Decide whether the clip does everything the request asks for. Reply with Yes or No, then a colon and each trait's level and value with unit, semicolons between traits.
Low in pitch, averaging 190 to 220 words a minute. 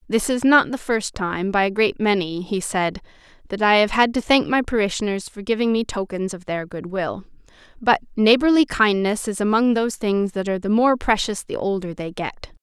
No: high, 210 Hz; fast, 205 wpm